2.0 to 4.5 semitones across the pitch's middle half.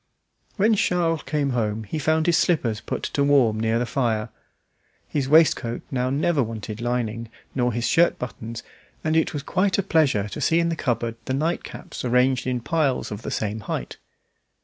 No: wide, 5.5 semitones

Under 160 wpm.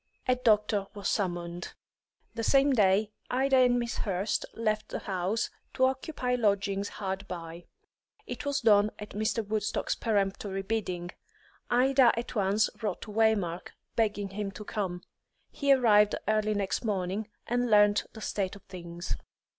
Yes: average, 145 wpm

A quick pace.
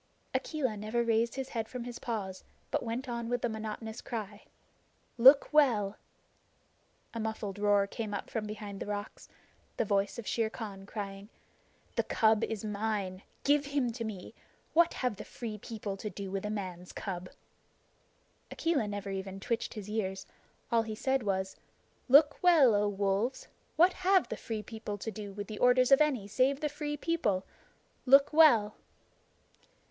No: average, 165 wpm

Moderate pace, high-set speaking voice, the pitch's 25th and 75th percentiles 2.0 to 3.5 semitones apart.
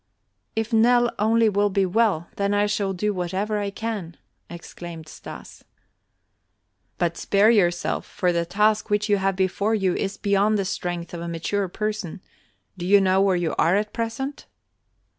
Yes: average, 165 wpm; high, 200 Hz; average, 3.1 semitones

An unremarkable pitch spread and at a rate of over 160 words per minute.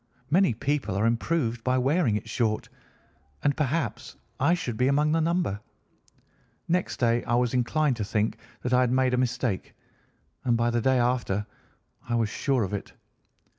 Yes: average, 3.7 semitones; average, 170 wpm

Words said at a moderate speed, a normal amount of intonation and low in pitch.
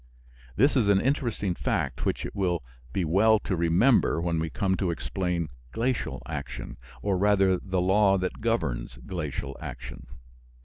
Yes: average, 150 wpm; average, 3.6 semitones; very low, 95 Hz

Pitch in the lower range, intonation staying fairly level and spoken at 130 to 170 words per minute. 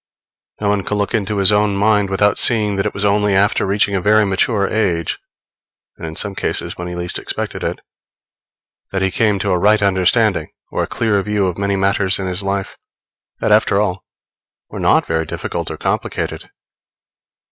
No: low, 100 Hz; narrow, 1.5 semitones; average, 190 wpm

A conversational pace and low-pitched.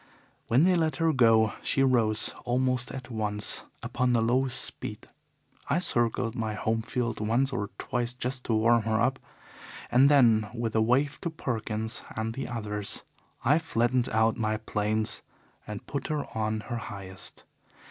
Yes: average, 160 wpm; low, 115 Hz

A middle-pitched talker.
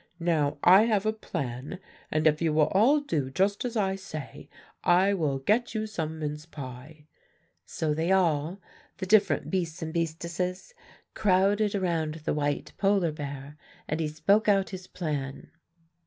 Yes: medium, 170 Hz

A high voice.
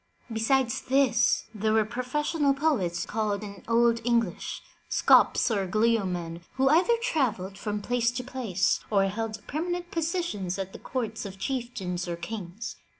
Yes: high, 225 Hz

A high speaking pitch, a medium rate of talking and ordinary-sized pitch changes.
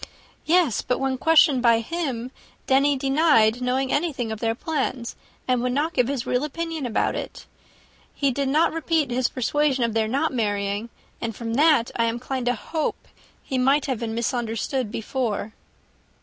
Yes: very high, 255 Hz; average, 170 wpm; average, 3.8 semitones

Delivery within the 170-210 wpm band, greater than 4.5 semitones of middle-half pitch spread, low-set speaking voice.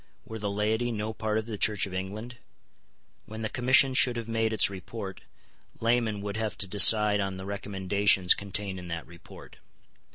No: average, 175 wpm; narrow, 2.4 semitones; low, 105 Hz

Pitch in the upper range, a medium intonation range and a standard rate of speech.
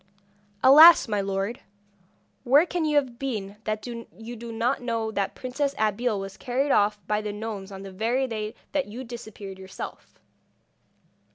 Yes: high, 225 Hz; average, 3.7 semitones; average, 165 wpm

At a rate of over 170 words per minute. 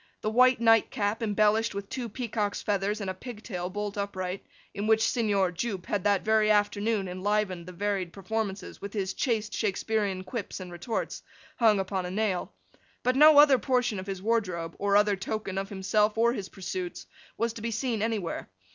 Yes: average, 180 wpm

